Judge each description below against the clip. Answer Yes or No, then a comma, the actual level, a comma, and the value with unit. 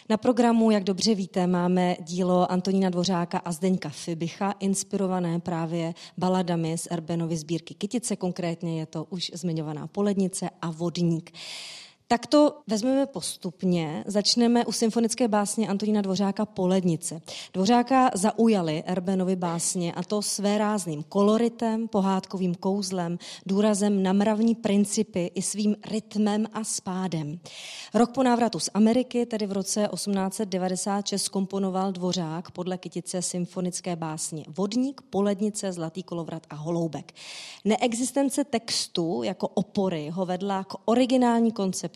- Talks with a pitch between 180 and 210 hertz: Yes, high, 190 Hz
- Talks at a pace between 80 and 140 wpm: Yes, average, 125 wpm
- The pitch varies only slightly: No, average, 3.5 semitones